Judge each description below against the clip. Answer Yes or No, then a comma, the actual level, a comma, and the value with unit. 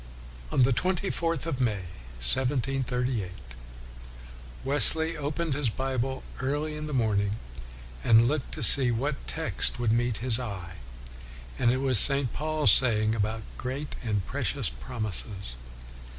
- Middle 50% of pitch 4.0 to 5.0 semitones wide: Yes, average, 4.3 semitones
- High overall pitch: No, low, 125 Hz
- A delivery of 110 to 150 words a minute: Yes, average, 140 wpm